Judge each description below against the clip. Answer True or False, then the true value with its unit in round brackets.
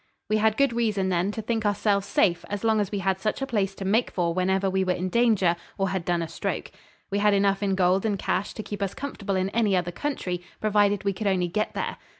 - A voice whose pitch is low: False (200 Hz)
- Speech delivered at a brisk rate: True (250 wpm)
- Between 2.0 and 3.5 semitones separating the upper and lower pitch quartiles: True (2.4 semitones)